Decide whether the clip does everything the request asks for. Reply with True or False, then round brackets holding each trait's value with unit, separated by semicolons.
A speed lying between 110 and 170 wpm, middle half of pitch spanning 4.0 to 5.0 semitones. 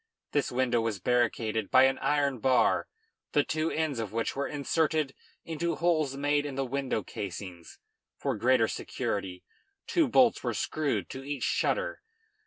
True (155 wpm; 4.4 semitones)